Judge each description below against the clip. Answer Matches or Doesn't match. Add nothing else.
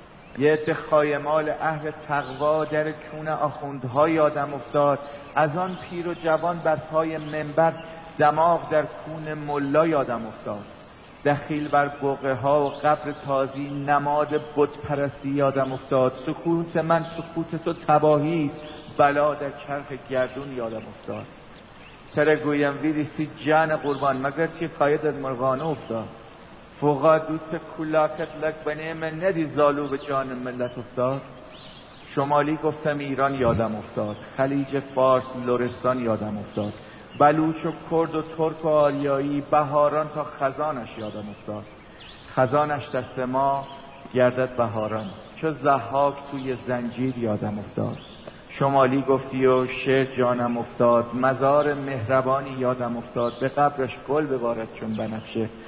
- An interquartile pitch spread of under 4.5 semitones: Matches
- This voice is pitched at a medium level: Matches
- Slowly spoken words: Matches